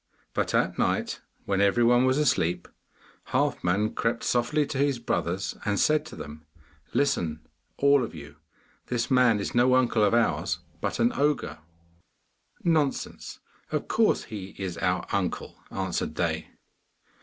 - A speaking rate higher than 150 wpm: No, average, 145 wpm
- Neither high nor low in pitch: No, low, 115 Hz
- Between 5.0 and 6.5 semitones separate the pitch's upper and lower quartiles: Yes, wide, 5.5 semitones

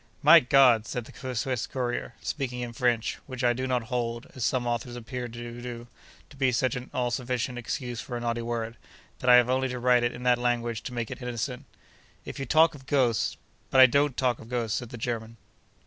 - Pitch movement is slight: Yes, narrow, 1.4 semitones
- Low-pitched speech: Yes, low, 125 Hz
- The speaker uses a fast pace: Yes, fast, 225 wpm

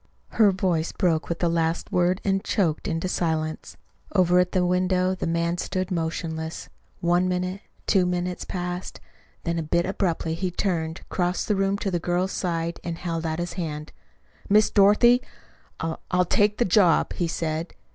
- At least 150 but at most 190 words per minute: Yes, average, 170 wpm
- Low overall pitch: No, medium, 180 Hz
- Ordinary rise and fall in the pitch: No, narrow, 2.0 semitones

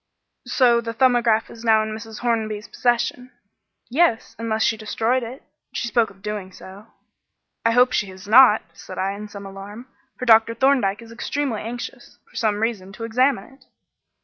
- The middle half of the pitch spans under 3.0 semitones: Yes, narrow, 2.4 semitones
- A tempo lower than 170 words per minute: No, average, 175 wpm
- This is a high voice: Yes, high, 225 Hz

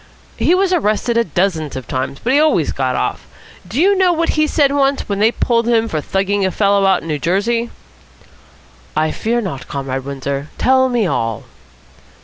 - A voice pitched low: No, high, 205 Hz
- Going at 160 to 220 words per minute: Yes, average, 185 wpm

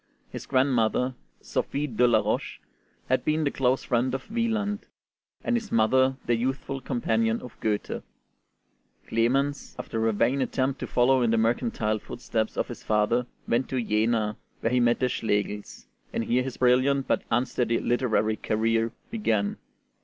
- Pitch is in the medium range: No, low, 120 Hz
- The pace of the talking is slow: No, average, 155 wpm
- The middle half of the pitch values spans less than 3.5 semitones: Yes, average, 2.9 semitones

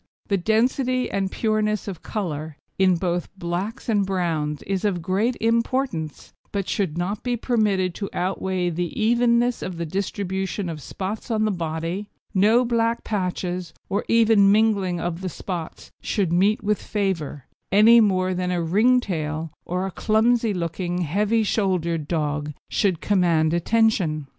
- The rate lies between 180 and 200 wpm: No, average, 150 wpm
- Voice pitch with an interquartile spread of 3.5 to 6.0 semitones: Yes, average, 3.9 semitones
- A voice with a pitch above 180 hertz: Yes, high, 190 Hz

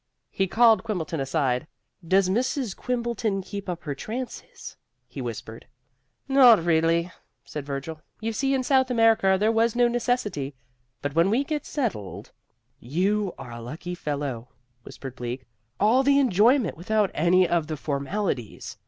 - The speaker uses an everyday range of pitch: No, wide, 8.3 semitones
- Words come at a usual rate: Yes, average, 150 wpm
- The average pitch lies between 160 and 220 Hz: Yes, medium, 185 Hz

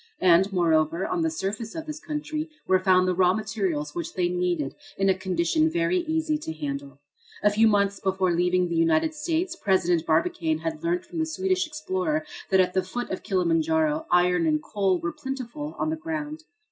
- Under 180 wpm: No, average, 190 wpm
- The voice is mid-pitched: No, high, 195 Hz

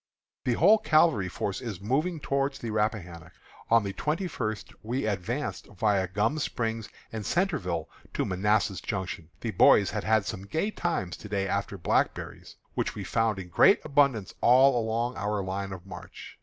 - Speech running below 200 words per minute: Yes, average, 170 wpm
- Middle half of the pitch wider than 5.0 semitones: Yes, wide, 5.5 semitones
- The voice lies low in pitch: Yes, low, 110 Hz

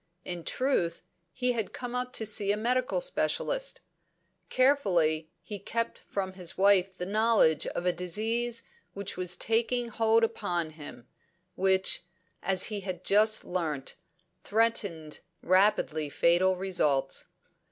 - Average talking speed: No, slow, 130 wpm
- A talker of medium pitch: No, high, 195 Hz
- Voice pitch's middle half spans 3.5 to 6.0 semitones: Yes, average, 4.4 semitones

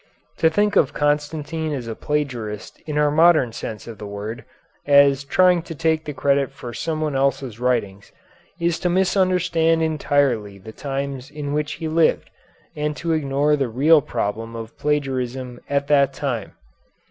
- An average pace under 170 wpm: Yes, average, 160 wpm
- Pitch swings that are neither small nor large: Yes, average, 3.9 semitones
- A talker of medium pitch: Yes, medium, 145 Hz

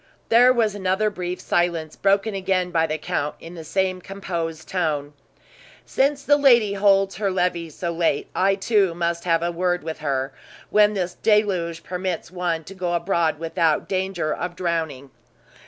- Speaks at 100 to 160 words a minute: No, average, 170 wpm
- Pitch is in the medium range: Yes, medium, 180 Hz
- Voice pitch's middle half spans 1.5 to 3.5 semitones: Yes, average, 2.9 semitones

